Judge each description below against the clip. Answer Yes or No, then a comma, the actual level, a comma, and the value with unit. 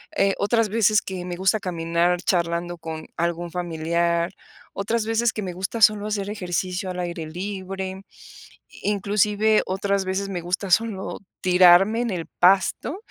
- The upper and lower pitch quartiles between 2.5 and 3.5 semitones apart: Yes, average, 2.9 semitones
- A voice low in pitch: No, high, 190 Hz